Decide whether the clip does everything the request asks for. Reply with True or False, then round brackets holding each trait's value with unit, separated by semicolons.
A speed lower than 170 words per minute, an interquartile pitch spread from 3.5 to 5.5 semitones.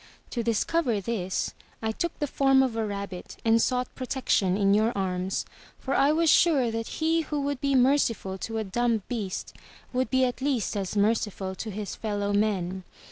False (185 wpm; 4.7 semitones)